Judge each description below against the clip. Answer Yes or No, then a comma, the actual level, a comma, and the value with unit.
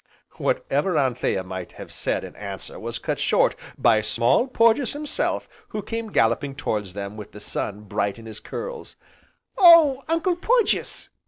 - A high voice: No, medium, 140 Hz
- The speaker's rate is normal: Yes, average, 155 wpm